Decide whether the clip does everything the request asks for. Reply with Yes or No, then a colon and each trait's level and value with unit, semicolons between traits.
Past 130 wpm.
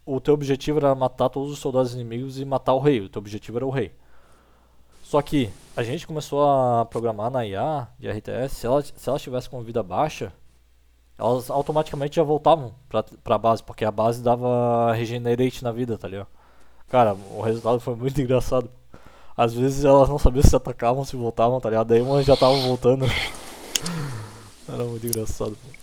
Yes: fast, 185 wpm